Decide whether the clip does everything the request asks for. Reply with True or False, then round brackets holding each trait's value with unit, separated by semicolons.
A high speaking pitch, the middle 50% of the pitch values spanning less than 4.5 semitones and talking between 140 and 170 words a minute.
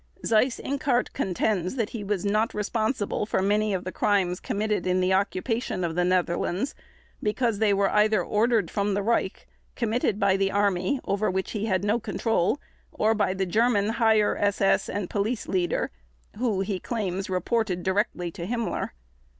True (205 Hz; 2.8 semitones; 165 wpm)